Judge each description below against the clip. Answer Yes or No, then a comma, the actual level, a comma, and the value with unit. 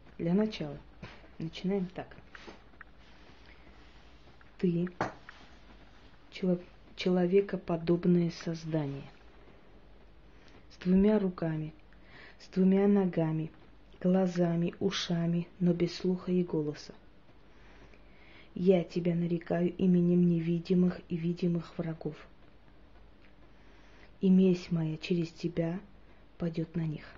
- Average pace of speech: No, slow, 80 wpm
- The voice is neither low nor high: Yes, medium, 175 Hz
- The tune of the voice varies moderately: No, narrow, 2.2 semitones